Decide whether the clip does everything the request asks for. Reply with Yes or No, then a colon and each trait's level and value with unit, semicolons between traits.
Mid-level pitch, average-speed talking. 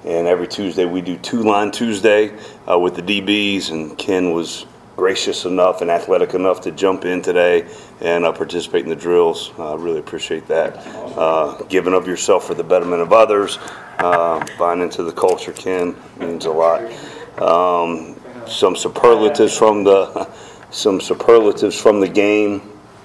No: low, 100 Hz; average, 165 wpm